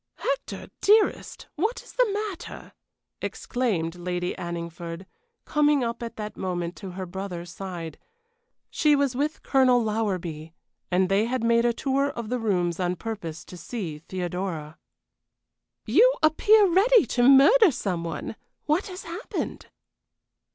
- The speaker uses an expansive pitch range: Yes, wide, 8.8 semitones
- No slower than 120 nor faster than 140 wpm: Yes, slow, 135 wpm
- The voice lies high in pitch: Yes, high, 220 Hz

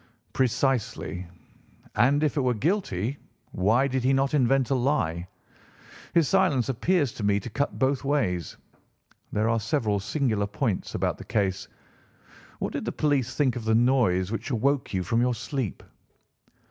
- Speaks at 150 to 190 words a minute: Yes, average, 160 wpm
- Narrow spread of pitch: No, average, 4.6 semitones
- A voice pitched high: No, low, 125 Hz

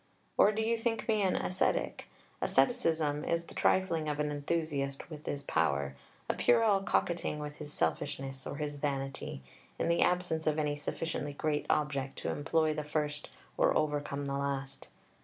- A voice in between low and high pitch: Yes, medium, 150 Hz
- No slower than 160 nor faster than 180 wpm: Yes, average, 165 wpm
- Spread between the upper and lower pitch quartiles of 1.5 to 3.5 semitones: Yes, average, 2.9 semitones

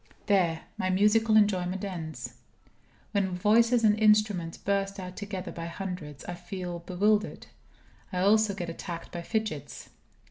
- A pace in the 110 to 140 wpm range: Yes, slow, 135 wpm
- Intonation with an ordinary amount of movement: Yes, average, 3.1 semitones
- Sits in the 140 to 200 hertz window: Yes, high, 190 Hz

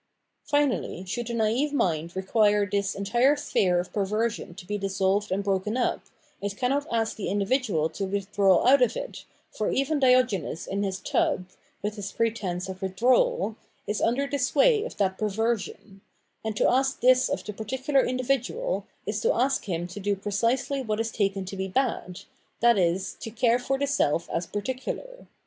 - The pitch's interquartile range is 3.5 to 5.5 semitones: Yes, average, 4.9 semitones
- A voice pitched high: Yes, high, 215 Hz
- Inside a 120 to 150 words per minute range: No, average, 175 wpm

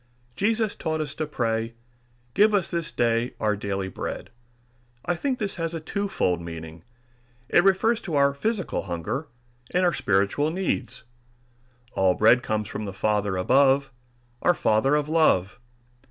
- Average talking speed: Yes, average, 150 wpm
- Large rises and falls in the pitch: Yes, wide, 9.0 semitones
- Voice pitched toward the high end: No, medium, 140 Hz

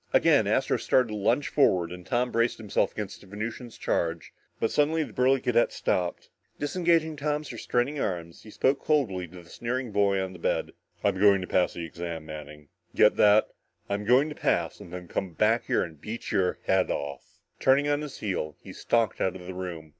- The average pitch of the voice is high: No, low, 105 Hz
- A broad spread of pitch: Yes, wide, 6.1 semitones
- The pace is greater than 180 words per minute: Yes, average, 200 wpm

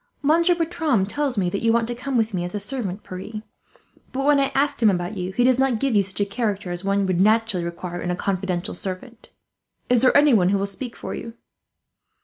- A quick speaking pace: Yes, fast, 225 wpm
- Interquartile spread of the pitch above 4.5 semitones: Yes, wide, 5.4 semitones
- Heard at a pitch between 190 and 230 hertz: Yes, high, 215 Hz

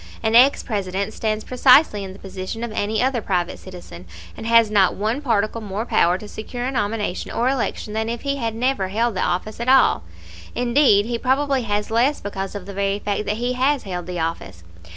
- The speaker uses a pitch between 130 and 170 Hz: No, high, 215 Hz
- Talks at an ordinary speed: No, fast, 210 wpm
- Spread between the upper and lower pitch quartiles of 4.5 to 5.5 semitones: No, average, 3.6 semitones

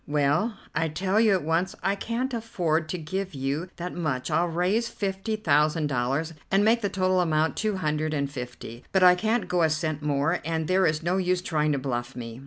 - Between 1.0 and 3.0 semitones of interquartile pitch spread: No, average, 4.2 semitones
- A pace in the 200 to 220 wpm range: Yes, fast, 205 wpm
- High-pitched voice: No, medium, 165 Hz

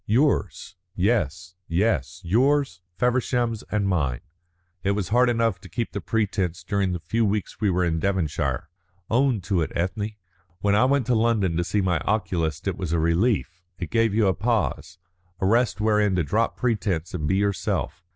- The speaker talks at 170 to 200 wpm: Yes, average, 180 wpm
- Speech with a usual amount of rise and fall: Yes, average, 4.4 semitones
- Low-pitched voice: Yes, low, 100 Hz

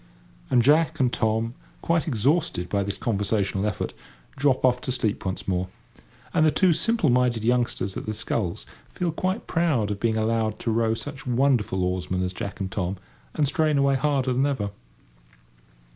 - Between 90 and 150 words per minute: No, average, 175 wpm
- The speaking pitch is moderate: No, low, 120 Hz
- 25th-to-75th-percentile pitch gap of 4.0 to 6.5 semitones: Yes, wide, 5.6 semitones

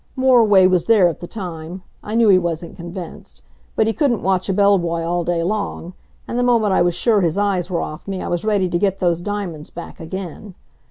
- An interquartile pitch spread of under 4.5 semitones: Yes, average, 3.1 semitones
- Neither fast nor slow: No, fast, 225 wpm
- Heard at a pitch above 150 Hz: Yes, medium, 185 Hz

